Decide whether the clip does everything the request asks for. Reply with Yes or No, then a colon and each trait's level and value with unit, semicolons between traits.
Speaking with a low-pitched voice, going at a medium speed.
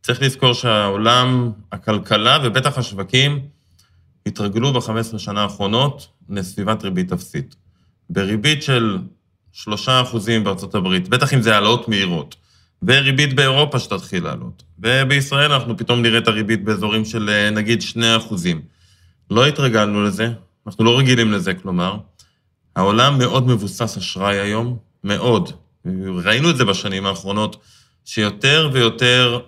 Yes: low, 110 Hz; average, 120 wpm